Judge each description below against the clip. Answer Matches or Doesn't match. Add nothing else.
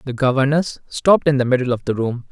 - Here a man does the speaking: Matches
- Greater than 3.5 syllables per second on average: Matches